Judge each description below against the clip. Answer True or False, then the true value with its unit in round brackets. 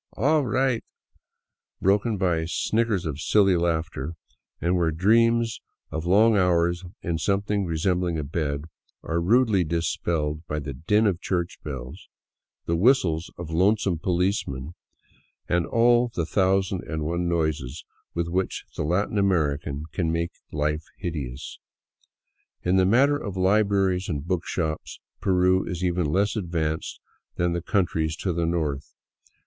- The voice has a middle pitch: False (85 Hz)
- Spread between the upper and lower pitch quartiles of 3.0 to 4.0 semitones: True (3.6 semitones)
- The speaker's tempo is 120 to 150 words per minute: True (140 wpm)